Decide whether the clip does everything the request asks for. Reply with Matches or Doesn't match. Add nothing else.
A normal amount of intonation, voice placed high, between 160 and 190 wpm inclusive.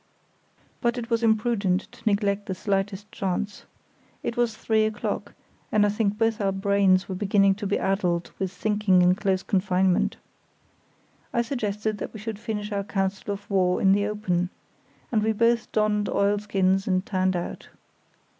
Doesn't match